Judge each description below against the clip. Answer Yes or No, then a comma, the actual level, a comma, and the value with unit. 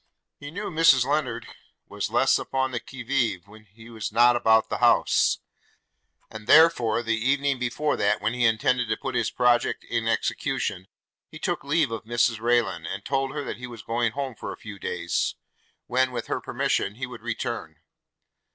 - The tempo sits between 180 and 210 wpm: Yes, average, 185 wpm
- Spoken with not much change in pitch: No, average, 3.0 semitones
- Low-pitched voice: Yes, low, 120 Hz